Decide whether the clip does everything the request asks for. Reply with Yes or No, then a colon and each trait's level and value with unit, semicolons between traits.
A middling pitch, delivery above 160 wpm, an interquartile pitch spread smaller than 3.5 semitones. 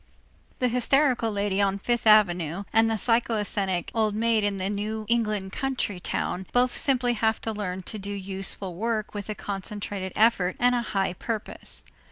No: high, 210 Hz; average, 170 wpm; average, 2.9 semitones